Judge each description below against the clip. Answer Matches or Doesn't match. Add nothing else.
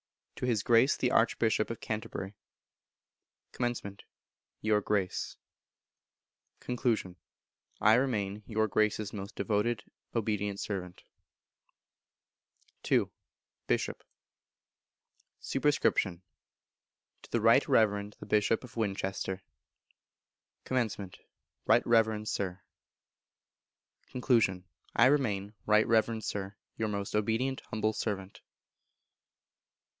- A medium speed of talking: Doesn't match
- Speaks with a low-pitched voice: Matches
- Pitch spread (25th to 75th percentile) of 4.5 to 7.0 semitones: Doesn't match